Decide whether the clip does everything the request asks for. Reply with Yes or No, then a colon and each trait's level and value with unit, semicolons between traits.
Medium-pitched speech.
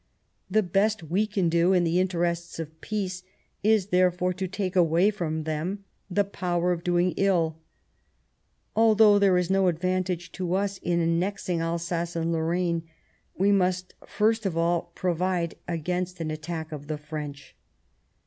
Yes: medium, 180 Hz